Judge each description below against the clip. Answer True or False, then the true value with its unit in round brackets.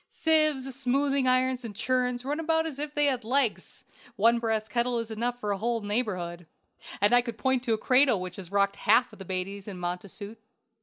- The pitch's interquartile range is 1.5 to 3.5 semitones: False (4.3 semitones)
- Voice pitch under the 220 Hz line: False (235 Hz)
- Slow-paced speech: False (200 wpm)